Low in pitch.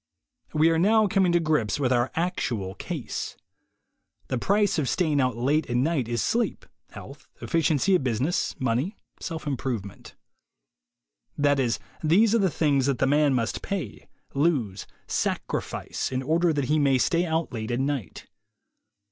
No: medium, 145 Hz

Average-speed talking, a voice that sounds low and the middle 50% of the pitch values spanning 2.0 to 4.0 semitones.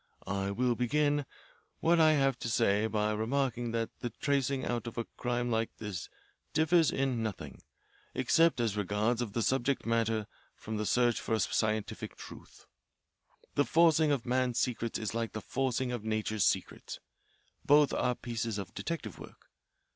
Yes: average, 160 wpm; low, 120 Hz; average, 3.7 semitones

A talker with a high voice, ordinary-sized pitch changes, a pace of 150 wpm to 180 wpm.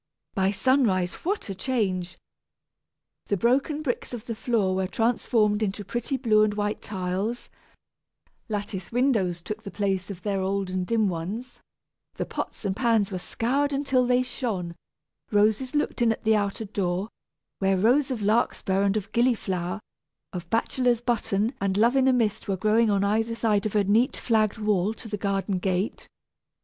Yes: high, 215 Hz; average, 3.5 semitones; average, 170 wpm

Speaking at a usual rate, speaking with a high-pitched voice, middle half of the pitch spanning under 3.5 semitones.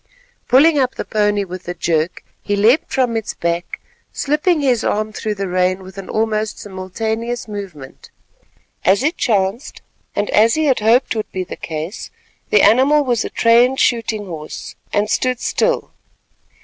No: average, 160 wpm; high, 215 Hz; average, 4.7 semitones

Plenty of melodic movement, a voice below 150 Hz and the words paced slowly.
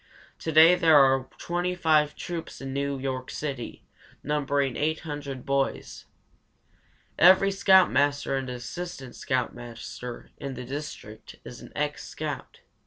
No: average, 3.3 semitones; medium, 140 Hz; slow, 115 wpm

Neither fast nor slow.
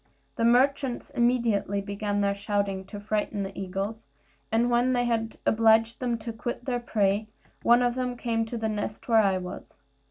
Yes: average, 180 wpm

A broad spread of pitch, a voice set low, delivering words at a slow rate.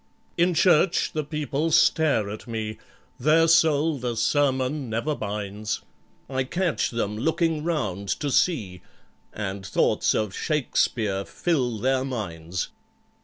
Yes: wide, 6.5 semitones; low, 130 Hz; slow, 120 wpm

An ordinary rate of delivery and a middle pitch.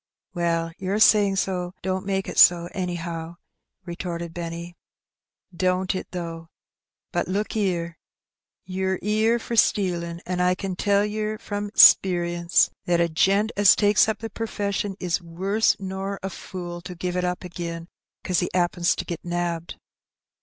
Yes: average, 155 wpm; medium, 180 Hz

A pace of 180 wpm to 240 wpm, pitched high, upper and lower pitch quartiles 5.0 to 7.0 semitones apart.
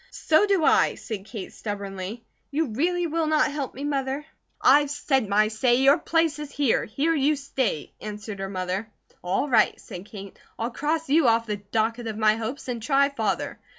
Yes: average, 185 wpm; very high, 250 Hz; wide, 5.5 semitones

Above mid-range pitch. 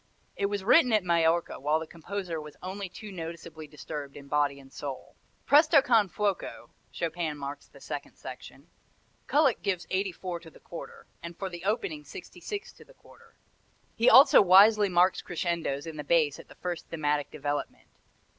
No: medium, 175 Hz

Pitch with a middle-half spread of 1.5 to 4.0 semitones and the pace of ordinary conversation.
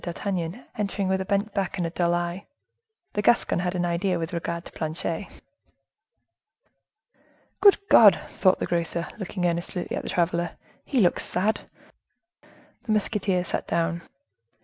Yes: average, 2.7 semitones; average, 150 wpm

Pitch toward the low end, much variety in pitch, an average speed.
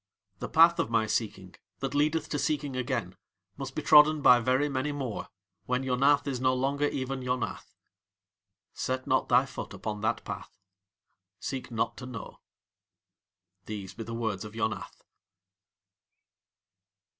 No: low, 130 Hz; average, 3.6 semitones; average, 145 wpm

